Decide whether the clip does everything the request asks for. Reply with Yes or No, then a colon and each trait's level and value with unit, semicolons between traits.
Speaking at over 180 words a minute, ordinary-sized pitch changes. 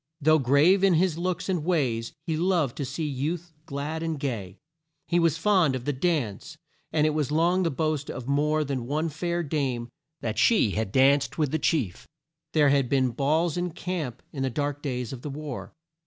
Yes: average, 200 wpm; average, 3.7 semitones